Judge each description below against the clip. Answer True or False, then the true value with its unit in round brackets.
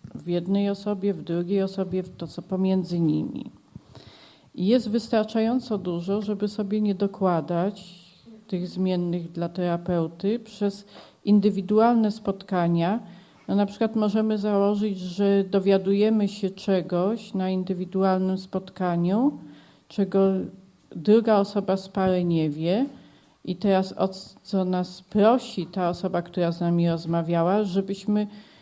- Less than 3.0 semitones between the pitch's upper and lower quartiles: True (2.5 semitones)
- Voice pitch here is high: True (195 Hz)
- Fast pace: False (115 wpm)